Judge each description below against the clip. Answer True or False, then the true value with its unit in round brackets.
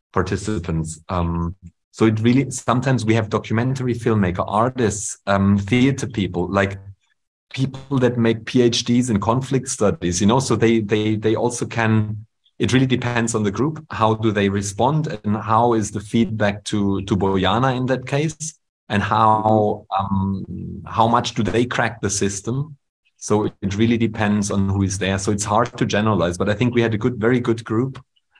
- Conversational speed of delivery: False (180 wpm)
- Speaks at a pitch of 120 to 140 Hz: False (110 Hz)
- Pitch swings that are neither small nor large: True (3.2 semitones)